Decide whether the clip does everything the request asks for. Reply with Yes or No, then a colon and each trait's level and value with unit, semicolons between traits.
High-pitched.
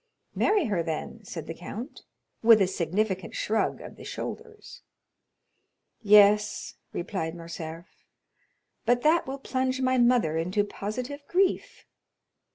Yes: high, 210 Hz